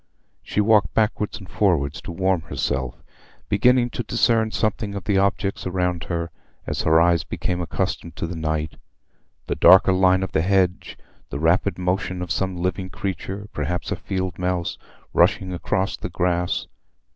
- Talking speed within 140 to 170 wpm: Yes, average, 150 wpm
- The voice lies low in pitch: Yes, very low, 90 Hz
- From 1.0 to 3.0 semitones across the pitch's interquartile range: Yes, narrow, 2.4 semitones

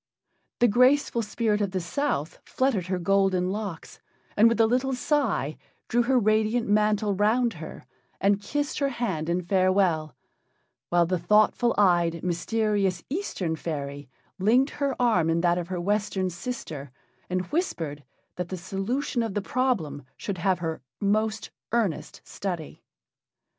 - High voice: Yes, high, 200 Hz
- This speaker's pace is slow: No, average, 145 wpm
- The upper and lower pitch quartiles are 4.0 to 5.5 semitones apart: Yes, average, 5.0 semitones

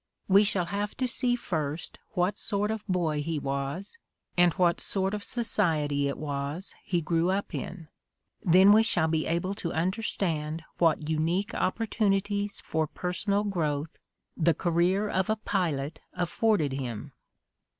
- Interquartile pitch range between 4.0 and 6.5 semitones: Yes, average, 4.4 semitones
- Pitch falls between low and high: Yes, medium, 175 Hz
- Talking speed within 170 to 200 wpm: No, average, 150 wpm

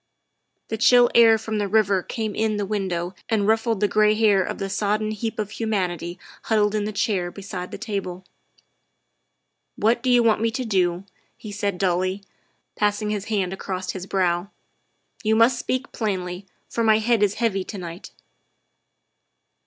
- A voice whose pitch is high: Yes, high, 205 Hz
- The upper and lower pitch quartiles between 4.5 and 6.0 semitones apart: No, average, 2.7 semitones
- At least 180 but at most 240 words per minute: Yes, average, 190 wpm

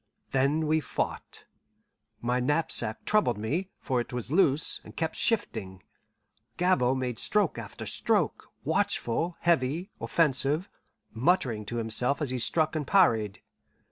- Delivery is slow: Yes, slow, 130 wpm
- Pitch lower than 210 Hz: Yes, medium, 140 Hz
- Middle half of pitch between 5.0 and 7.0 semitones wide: Yes, wide, 5.4 semitones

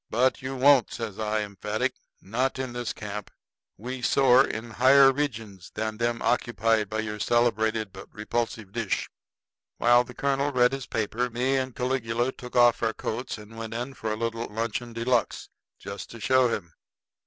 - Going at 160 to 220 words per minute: Yes, average, 175 wpm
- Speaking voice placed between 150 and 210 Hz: No, low, 115 Hz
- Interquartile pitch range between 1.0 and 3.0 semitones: Yes, narrow, 2.5 semitones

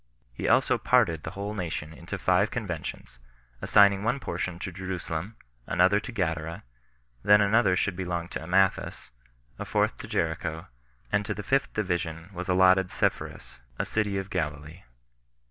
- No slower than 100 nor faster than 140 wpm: No, average, 150 wpm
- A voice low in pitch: Yes, very low, 95 Hz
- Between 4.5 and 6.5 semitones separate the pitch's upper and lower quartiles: No, average, 3.6 semitones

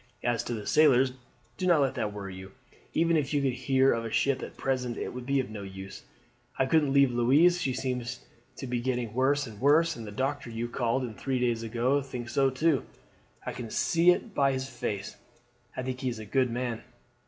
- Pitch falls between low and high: No, low, 130 Hz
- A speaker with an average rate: No, fast, 230 wpm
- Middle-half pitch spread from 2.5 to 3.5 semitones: Yes, average, 2.8 semitones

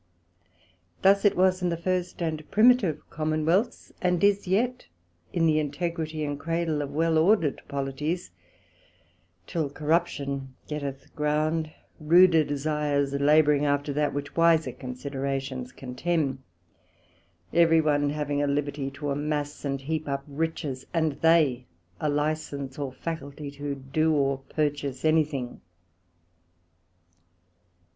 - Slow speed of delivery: Yes, slow, 120 wpm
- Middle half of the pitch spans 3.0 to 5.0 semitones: No, narrow, 2.6 semitones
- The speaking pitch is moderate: Yes, medium, 150 Hz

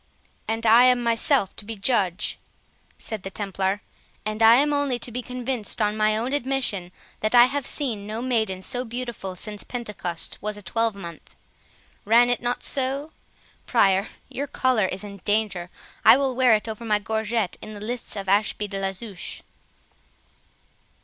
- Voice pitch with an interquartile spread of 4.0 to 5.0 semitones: No, average, 3.4 semitones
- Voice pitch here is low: No, high, 220 Hz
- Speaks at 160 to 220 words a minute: Yes, average, 165 wpm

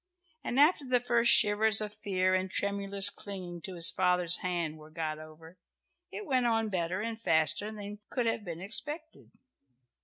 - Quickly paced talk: No, average, 165 wpm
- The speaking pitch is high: Yes, high, 200 Hz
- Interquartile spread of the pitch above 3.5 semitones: Yes, average, 4.3 semitones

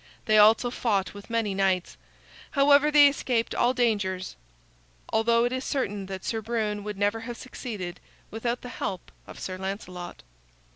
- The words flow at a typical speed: Yes, average, 155 wpm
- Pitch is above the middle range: Yes, high, 220 Hz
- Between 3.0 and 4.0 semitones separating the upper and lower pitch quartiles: Yes, average, 3.7 semitones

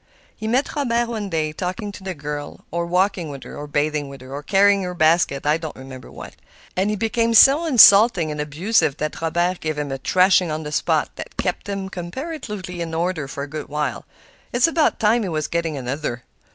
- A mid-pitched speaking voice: Yes, medium, 170 Hz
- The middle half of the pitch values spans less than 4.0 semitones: No, average, 5.3 semitones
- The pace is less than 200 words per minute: No, fast, 205 wpm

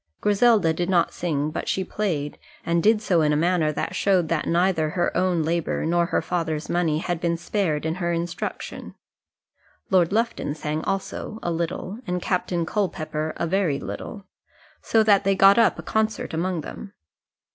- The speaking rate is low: No, average, 175 wpm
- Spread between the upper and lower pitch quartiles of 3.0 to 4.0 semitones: Yes, average, 3.3 semitones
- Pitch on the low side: No, medium, 175 Hz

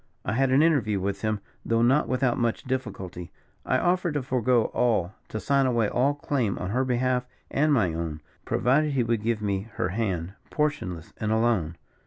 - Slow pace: No, average, 185 wpm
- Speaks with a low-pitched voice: Yes, low, 115 Hz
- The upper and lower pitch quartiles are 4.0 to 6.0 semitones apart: Yes, average, 4.7 semitones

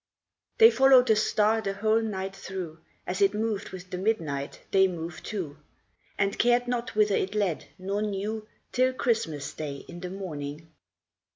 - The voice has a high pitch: Yes, high, 195 Hz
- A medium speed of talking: Yes, average, 165 wpm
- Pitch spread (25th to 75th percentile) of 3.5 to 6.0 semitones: Yes, average, 3.8 semitones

